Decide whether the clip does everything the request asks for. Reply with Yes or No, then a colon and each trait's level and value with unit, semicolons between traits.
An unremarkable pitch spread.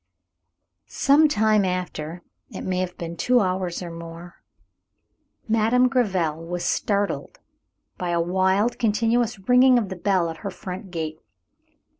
Yes: average, 4.5 semitones